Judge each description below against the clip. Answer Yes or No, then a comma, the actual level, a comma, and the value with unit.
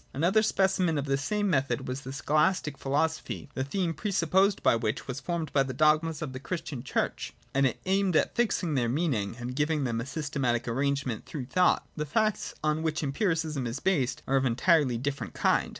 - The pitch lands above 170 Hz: No, medium, 145 Hz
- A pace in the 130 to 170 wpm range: No, fast, 205 wpm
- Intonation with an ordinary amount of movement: Yes, average, 4.1 semitones